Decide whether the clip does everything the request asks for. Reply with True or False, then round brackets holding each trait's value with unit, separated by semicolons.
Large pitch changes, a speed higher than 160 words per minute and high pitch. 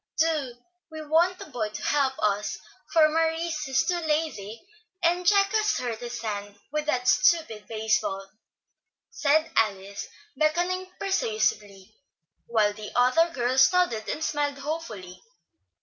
False (7.1 semitones; 135 wpm; 280 Hz)